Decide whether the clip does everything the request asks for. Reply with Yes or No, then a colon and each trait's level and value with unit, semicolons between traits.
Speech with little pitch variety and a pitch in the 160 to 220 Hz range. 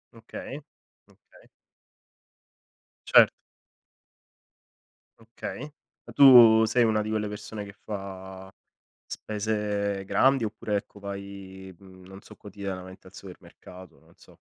No: narrow, 2.3 semitones; low, 100 Hz